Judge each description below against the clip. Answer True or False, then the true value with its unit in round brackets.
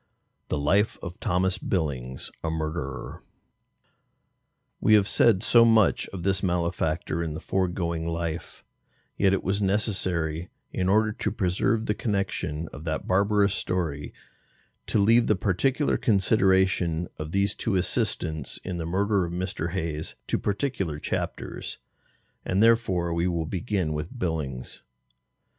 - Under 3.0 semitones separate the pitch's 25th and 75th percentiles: False (3.6 semitones)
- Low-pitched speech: True (90 Hz)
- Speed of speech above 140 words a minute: False (135 wpm)